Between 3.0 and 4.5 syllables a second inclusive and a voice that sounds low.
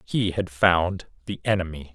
Yes: 4.3 syllables/s; very low, 90 Hz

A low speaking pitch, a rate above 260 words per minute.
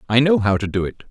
Yes: low, 115 Hz; fast, 325 wpm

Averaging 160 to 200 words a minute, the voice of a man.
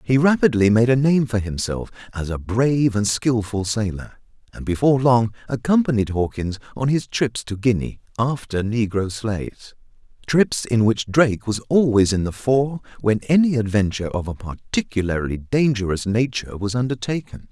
No: average, 150 wpm; male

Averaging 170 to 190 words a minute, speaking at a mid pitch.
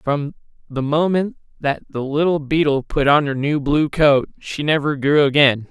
Yes: average, 180 wpm; medium, 145 Hz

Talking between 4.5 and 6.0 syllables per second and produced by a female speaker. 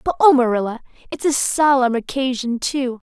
Yes: 5.1 syllables/s; female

